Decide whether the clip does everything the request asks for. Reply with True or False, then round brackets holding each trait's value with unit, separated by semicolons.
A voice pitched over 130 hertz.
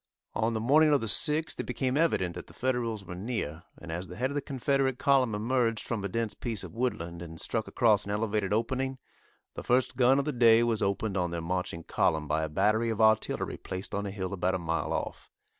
False (110 Hz)